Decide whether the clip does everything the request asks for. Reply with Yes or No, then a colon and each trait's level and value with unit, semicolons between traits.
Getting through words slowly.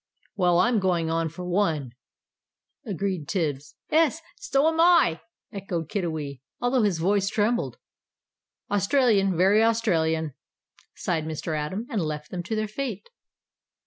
Yes: slow, 130 wpm